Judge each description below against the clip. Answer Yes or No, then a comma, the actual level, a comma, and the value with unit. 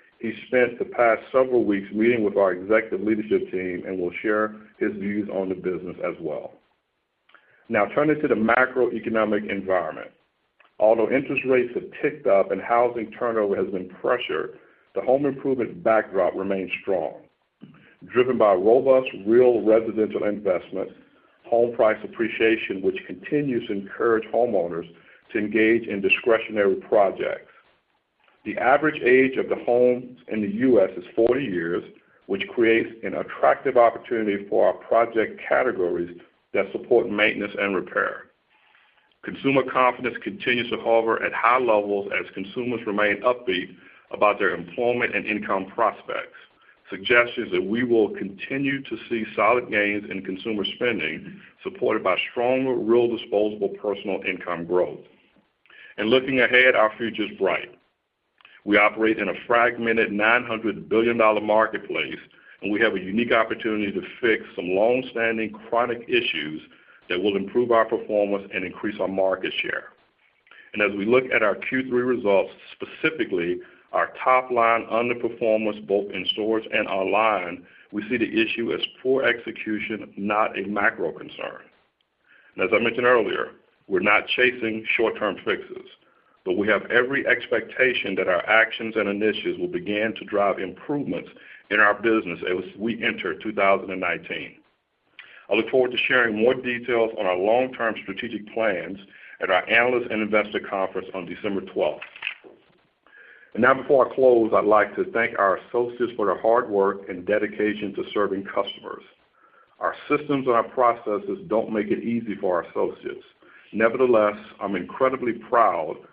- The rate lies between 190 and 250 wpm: No, average, 145 wpm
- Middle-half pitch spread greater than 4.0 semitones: No, average, 3.3 semitones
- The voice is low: Yes, low, 115 Hz